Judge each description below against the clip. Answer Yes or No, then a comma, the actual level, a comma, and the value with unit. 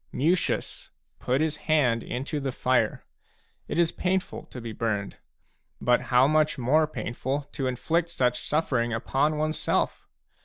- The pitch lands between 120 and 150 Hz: Yes, low, 135 Hz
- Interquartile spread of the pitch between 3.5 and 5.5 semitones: Yes, average, 4.0 semitones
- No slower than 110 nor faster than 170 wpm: Yes, average, 140 wpm